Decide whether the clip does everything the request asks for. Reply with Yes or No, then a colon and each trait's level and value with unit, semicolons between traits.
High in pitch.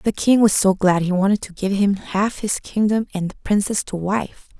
Yes: high, 200 Hz